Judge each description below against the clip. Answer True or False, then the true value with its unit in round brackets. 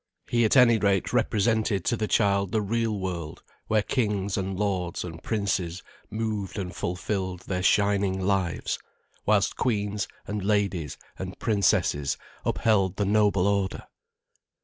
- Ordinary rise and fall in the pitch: False (2.2 semitones)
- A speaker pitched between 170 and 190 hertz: False (100 Hz)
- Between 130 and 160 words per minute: True (135 wpm)